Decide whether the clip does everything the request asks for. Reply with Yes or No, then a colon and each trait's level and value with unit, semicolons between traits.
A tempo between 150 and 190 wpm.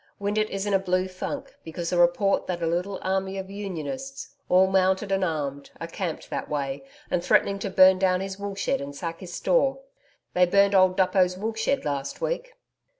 No: average, 200 wpm